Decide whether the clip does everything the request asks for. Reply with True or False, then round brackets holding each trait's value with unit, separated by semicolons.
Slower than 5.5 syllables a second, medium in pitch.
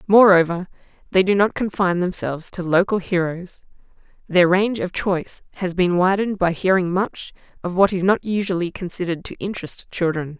False (5.6 syllables/s; 180 Hz)